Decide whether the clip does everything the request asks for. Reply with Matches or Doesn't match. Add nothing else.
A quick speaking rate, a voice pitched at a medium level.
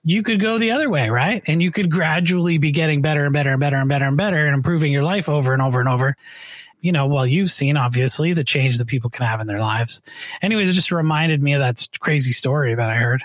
Matches